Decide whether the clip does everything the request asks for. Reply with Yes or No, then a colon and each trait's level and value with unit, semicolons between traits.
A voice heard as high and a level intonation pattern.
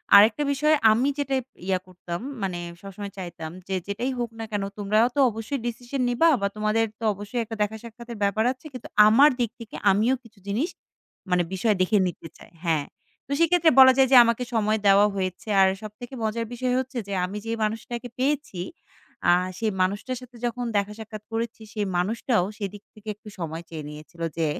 No: high, 220 Hz; average, 3.7 semitones